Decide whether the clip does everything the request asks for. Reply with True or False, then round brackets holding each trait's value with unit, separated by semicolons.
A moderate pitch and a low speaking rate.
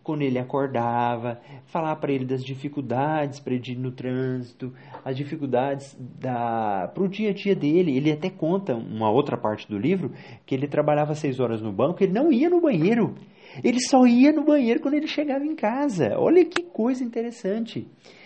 False (145 Hz; 185 wpm)